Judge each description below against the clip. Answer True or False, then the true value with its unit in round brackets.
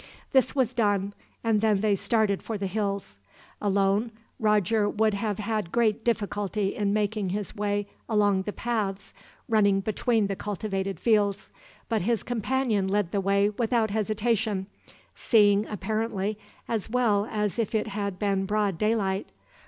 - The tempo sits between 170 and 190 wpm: False (145 wpm)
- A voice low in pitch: False (210 Hz)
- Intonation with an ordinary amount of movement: False (1.8 semitones)